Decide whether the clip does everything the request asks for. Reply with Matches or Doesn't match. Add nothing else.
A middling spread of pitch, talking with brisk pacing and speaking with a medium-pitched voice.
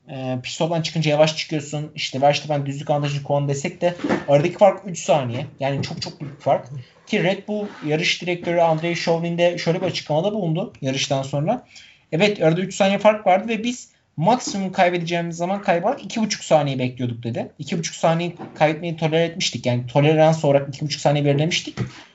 Matches